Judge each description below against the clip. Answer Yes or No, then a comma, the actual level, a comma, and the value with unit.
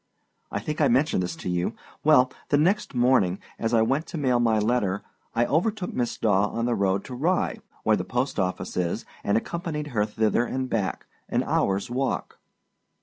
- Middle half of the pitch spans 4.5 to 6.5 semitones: Yes, wide, 5.6 semitones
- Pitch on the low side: Yes, low, 120 Hz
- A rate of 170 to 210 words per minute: Yes, average, 190 wpm